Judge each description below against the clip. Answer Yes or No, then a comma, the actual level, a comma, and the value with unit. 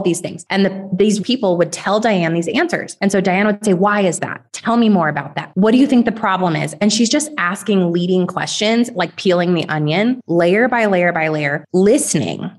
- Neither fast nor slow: No, fast, 225 wpm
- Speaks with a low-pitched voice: No, high, 190 Hz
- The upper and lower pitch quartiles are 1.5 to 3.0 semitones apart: No, average, 3.6 semitones